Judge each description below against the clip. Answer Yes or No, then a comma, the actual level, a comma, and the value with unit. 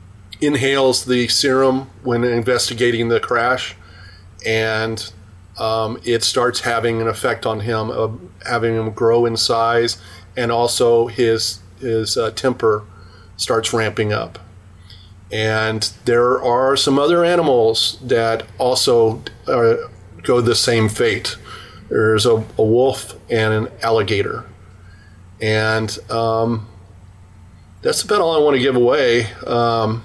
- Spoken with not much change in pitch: No, average, 3.2 semitones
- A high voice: No, low, 110 Hz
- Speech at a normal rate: No, slow, 125 wpm